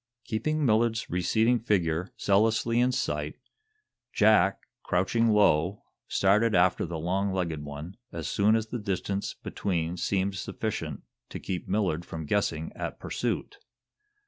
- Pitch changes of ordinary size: Yes, average, 4.3 semitones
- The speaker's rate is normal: No, slow, 130 wpm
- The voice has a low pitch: Yes, low, 100 Hz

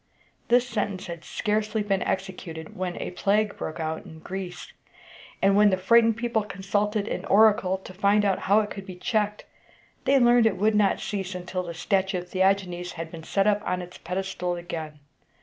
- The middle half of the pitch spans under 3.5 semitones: Yes, average, 2.8 semitones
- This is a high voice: Yes, high, 195 Hz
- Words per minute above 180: Yes, average, 190 wpm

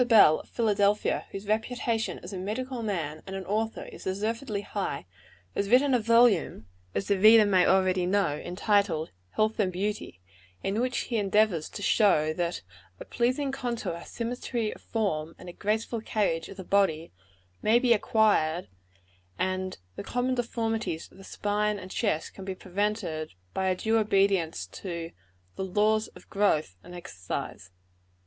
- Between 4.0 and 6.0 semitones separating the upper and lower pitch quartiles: No, average, 3.6 semitones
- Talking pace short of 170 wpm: Yes, average, 155 wpm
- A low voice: No, high, 205 Hz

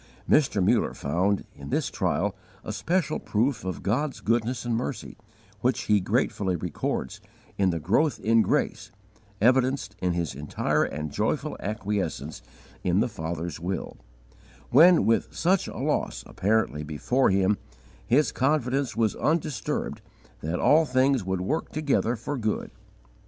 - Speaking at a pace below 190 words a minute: Yes, average, 140 wpm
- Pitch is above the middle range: No, low, 110 Hz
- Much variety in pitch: Yes, wide, 6.6 semitones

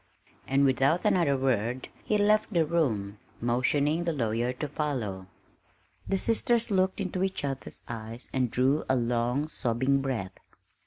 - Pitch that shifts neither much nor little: No, wide, 5.9 semitones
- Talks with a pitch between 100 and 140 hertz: Yes, low, 135 Hz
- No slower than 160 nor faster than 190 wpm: No, average, 145 wpm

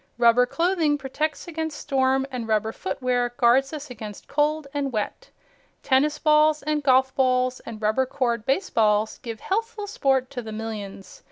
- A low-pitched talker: No, very high, 260 Hz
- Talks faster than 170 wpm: No, average, 155 wpm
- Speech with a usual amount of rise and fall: Yes, average, 4.4 semitones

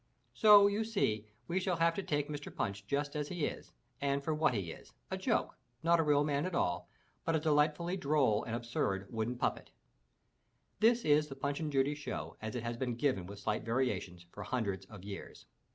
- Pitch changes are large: Yes, wide, 6.4 semitones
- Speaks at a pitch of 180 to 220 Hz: No, medium, 140 Hz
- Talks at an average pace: No, fast, 210 wpm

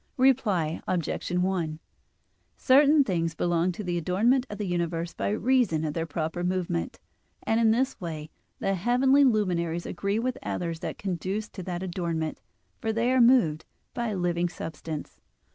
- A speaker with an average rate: Yes, average, 160 wpm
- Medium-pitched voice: Yes, medium, 180 Hz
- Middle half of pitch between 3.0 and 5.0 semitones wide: No, wide, 5.4 semitones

